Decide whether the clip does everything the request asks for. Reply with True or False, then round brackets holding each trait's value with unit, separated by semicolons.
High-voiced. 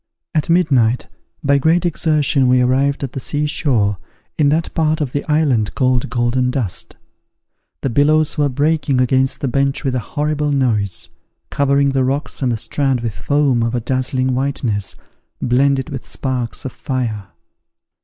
False (135 Hz)